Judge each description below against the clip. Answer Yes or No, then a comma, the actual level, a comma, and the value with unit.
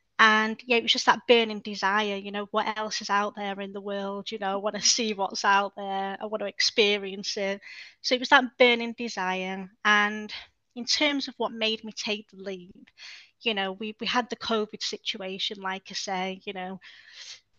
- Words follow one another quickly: Yes, fast, 210 wpm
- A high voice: Yes, high, 210 Hz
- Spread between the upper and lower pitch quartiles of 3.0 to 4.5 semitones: No, narrow, 2.5 semitones